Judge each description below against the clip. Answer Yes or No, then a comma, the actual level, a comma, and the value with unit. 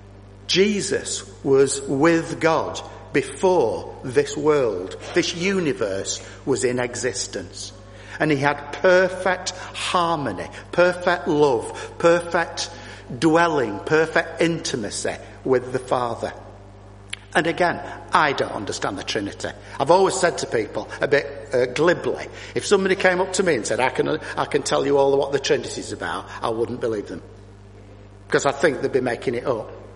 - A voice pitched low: No, medium, 145 Hz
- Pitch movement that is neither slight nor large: No, wide, 8.7 semitones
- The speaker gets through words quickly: No, average, 150 wpm